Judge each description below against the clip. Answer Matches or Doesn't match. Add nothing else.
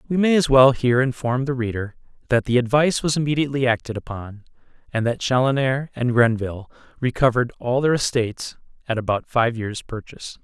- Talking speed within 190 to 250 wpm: Doesn't match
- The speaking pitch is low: Matches